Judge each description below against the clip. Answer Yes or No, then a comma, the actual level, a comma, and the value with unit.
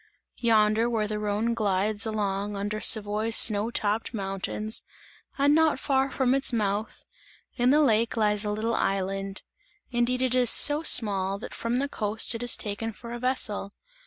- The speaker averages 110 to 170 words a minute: Yes, average, 165 wpm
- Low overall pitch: No, high, 220 Hz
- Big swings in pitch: No, average, 2.7 semitones